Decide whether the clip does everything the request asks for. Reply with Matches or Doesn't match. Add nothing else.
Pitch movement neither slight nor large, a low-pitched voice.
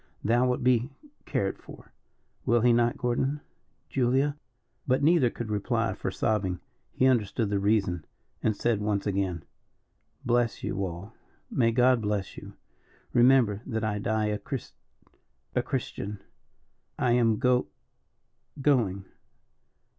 Matches